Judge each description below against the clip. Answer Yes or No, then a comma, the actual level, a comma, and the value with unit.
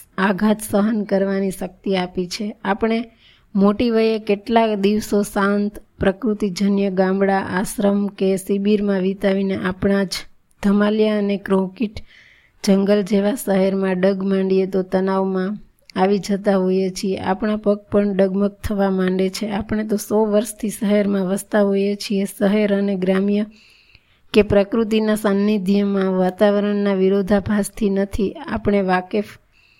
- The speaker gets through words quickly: No, average, 120 wpm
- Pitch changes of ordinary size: No, narrow, 1.3 semitones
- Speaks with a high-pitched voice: Yes, high, 200 Hz